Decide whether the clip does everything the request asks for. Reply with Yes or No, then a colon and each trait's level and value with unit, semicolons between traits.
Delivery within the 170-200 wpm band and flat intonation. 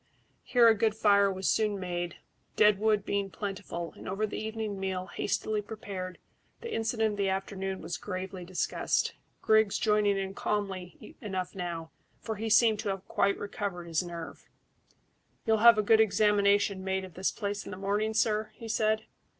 Yes: average, 175 wpm; narrow, 2.2 semitones